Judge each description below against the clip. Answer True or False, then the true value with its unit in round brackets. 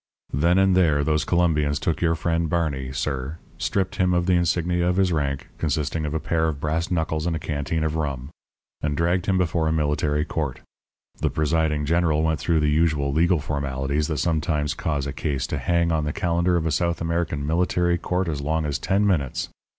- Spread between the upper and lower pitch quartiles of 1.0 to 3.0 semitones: True (2.6 semitones)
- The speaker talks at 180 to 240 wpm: True (205 wpm)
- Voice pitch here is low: True (80 Hz)